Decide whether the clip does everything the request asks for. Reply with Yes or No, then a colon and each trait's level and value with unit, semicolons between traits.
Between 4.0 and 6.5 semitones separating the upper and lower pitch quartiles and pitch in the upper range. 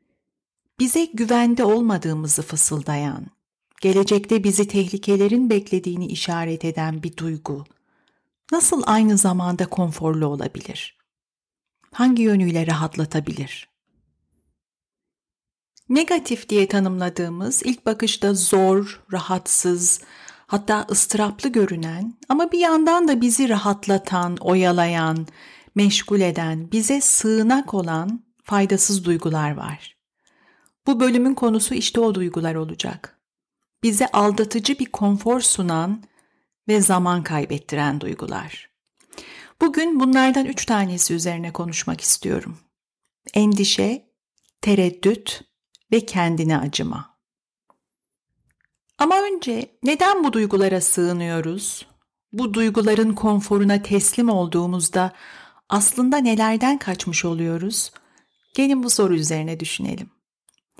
Yes: average, 5.2 semitones; high, 200 Hz